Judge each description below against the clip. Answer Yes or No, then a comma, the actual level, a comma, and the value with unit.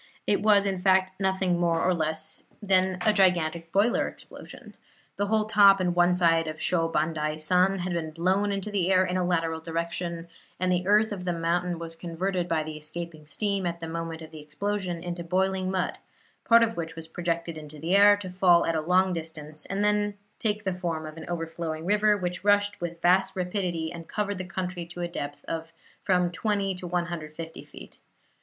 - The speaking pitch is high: No, medium, 175 Hz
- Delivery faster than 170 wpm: Yes, average, 200 wpm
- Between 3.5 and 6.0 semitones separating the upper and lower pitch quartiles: No, narrow, 2.6 semitones